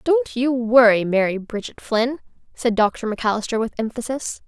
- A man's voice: No, female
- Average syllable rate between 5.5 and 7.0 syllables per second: No, 5.1 syllables/s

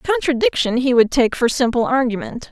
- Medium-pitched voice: No, very high, 260 Hz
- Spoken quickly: No, average, 165 wpm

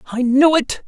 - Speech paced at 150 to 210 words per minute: Yes, fast, 205 wpm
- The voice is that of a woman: No, male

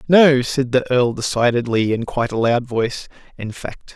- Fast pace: No, average, 165 wpm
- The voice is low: Yes, low, 125 Hz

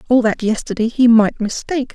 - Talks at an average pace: Yes, average, 185 wpm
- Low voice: No, high, 230 Hz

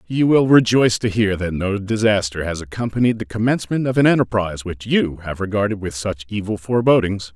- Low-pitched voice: Yes, low, 105 Hz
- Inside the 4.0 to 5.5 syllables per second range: No, 5.9 syllables/s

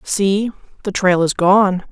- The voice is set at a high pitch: Yes, high, 195 Hz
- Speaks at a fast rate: No, average, 155 wpm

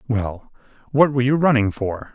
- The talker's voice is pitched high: No, low, 120 Hz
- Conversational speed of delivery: Yes, average, 170 wpm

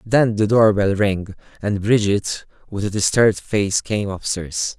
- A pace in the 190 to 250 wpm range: No, average, 175 wpm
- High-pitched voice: No, low, 105 Hz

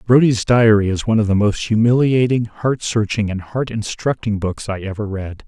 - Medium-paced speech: Yes, average, 185 wpm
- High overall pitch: No, low, 110 Hz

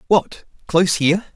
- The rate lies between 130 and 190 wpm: Yes, slow, 135 wpm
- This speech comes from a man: Yes, male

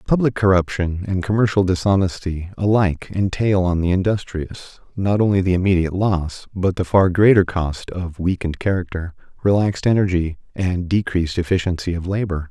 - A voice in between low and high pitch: No, very low, 95 Hz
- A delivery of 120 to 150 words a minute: Yes, average, 145 wpm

